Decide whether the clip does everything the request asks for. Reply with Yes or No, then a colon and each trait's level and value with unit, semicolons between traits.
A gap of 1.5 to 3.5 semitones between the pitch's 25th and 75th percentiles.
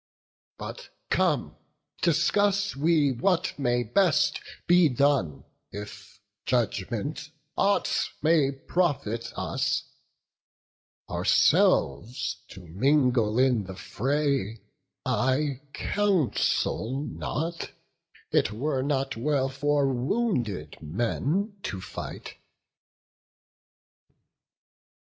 No: average, 5.2 semitones